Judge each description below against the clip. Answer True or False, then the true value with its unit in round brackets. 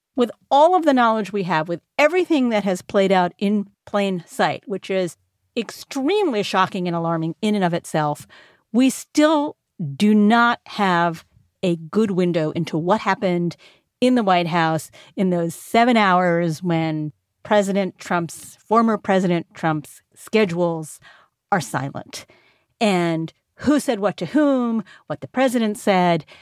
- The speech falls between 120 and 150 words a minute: True (145 wpm)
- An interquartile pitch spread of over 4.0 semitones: True (4.6 semitones)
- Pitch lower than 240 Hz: True (190 Hz)